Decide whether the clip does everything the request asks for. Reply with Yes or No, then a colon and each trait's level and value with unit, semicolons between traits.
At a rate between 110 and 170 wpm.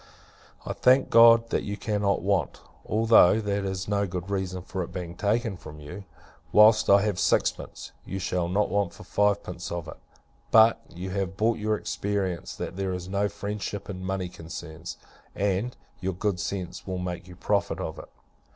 No: average, 180 wpm